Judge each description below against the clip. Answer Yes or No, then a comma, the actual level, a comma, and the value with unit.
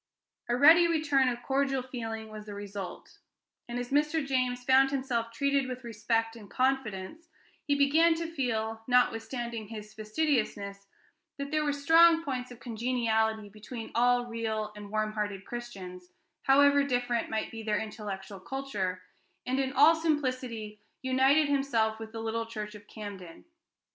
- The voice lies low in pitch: No, high, 240 Hz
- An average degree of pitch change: Yes, average, 4.1 semitones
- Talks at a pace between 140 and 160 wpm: Yes, average, 150 wpm